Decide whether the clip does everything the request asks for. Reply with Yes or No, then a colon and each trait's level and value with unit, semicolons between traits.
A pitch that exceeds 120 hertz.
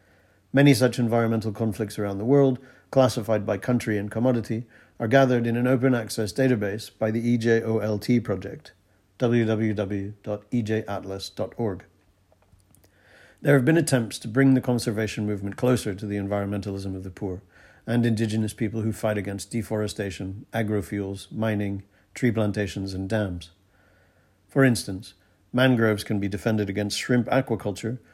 No: low, 110 Hz